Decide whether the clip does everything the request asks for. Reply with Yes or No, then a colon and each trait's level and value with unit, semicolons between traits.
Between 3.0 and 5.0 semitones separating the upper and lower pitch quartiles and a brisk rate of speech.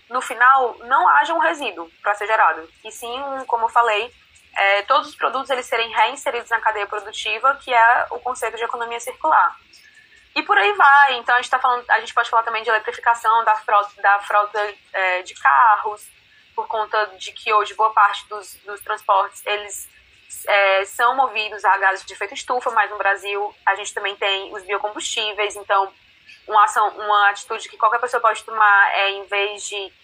Yes: average, 3.3 semitones; fast, 190 wpm